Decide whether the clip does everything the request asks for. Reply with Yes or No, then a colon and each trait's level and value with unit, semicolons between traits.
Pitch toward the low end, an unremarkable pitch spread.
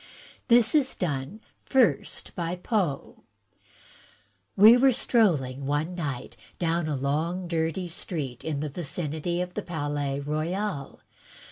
No: medium, 165 Hz; average, 4.4 semitones